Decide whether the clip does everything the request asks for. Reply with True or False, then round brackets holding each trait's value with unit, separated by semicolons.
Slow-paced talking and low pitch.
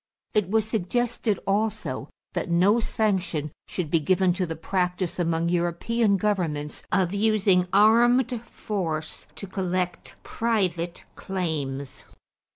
False (115 wpm; 185 Hz)